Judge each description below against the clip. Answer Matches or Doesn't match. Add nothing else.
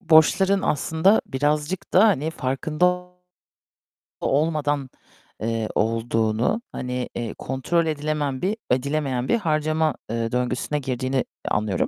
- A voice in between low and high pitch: Matches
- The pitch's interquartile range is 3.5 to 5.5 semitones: Matches